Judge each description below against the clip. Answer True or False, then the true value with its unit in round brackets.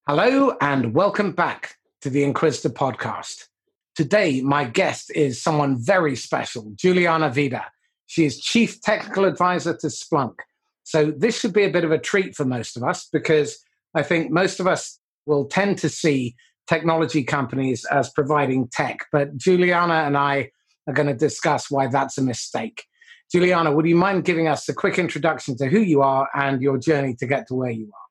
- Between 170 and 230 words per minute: True (185 wpm)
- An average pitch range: True (4.3 semitones)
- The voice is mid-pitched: True (150 Hz)